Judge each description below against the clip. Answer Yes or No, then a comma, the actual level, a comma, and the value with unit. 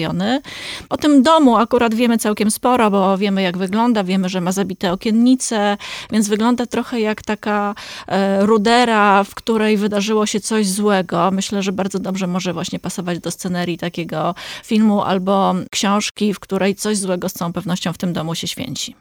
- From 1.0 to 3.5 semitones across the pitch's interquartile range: Yes, average, 2.9 semitones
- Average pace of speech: No, fast, 165 wpm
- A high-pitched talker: Yes, high, 205 Hz